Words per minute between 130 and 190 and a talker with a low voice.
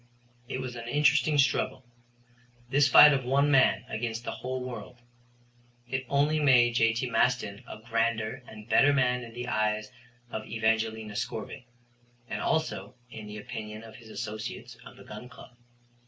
Yes: average, 155 wpm; low, 120 Hz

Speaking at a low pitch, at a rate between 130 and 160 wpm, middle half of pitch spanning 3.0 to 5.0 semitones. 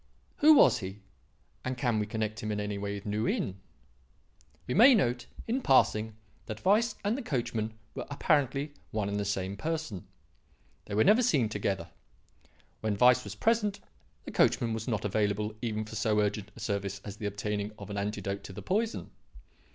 No: low, 110 Hz; average, 180 wpm; average, 4.7 semitones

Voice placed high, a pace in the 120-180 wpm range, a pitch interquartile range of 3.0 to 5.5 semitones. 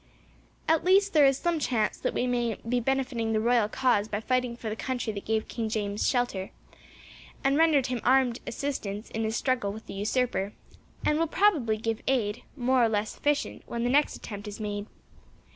No: high, 240 Hz; average, 195 wpm; average, 3.7 semitones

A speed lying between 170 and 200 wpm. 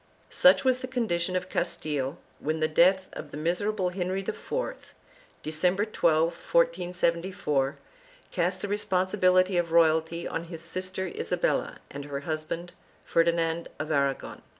No: slow, 135 wpm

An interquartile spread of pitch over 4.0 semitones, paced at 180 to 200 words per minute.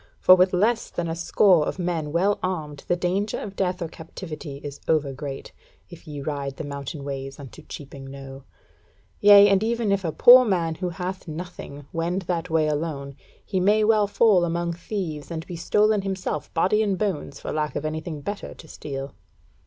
Yes: average, 4.5 semitones; average, 190 wpm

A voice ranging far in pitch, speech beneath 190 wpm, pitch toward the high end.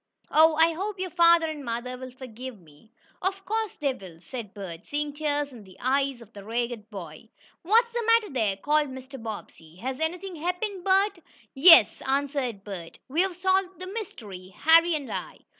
Yes: wide, 7.9 semitones; average, 175 wpm; very high, 280 Hz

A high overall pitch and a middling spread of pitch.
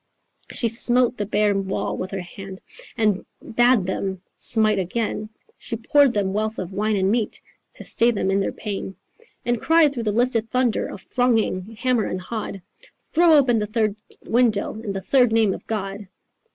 Yes: high, 215 Hz; average, 3.5 semitones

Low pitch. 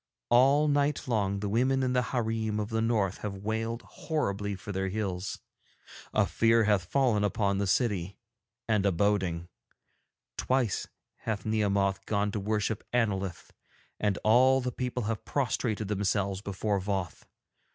Yes: low, 105 Hz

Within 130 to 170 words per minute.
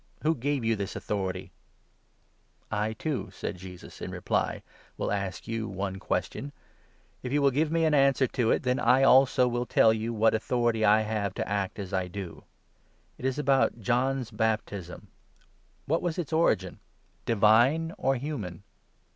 No: average, 180 wpm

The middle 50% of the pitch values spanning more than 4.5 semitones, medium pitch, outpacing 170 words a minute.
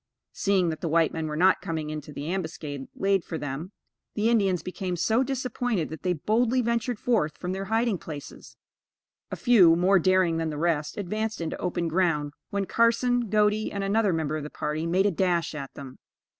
Yes: average, 5.0 semitones; medium, 180 Hz; average, 195 wpm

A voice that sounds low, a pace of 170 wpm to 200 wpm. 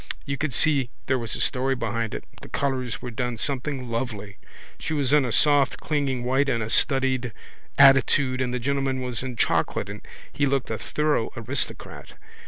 Yes: low, 130 Hz; average, 185 wpm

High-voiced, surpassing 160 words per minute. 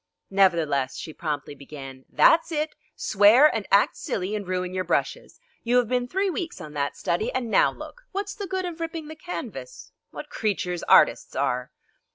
Yes: high, 210 Hz; average, 180 wpm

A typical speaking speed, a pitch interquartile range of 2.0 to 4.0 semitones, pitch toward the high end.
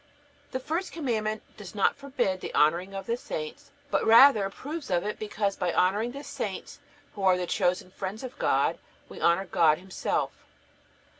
No: average, 170 wpm; average, 4.9 semitones; high, 200 Hz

